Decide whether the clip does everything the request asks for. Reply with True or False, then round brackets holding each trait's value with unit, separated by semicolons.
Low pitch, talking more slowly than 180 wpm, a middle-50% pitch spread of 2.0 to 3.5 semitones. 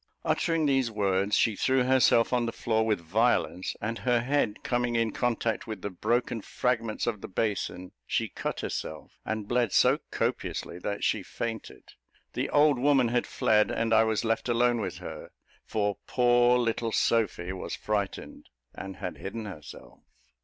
True (115 Hz; 165 wpm; 2.9 semitones)